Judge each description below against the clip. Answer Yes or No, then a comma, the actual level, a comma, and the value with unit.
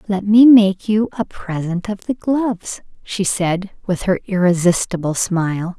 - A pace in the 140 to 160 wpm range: Yes, average, 155 wpm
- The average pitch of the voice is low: No, high, 195 Hz